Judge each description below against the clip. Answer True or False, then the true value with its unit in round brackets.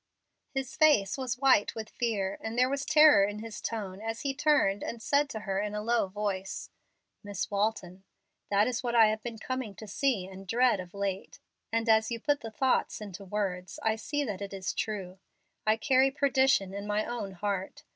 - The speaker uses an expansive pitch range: False (4.2 semitones)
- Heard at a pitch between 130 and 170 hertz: False (215 Hz)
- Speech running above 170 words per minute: True (200 wpm)